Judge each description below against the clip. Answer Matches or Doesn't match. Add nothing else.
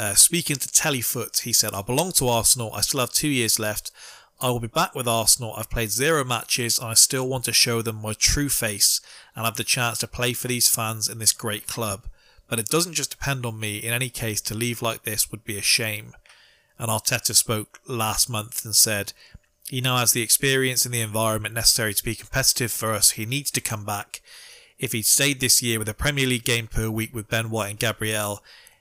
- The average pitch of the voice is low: Matches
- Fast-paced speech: Matches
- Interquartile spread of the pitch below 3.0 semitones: Matches